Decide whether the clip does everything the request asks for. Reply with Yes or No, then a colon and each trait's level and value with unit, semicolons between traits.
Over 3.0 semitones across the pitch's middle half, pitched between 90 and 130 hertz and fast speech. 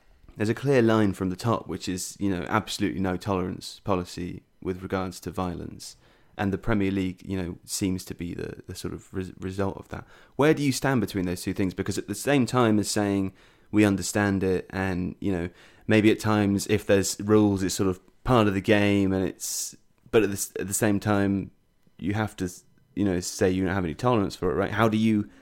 No: narrow, 2.4 semitones; low, 100 Hz; fast, 225 wpm